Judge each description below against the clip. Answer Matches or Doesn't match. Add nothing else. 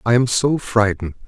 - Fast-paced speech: Doesn't match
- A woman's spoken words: Doesn't match